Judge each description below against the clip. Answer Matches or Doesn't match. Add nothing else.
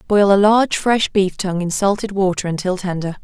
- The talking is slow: Doesn't match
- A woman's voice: Matches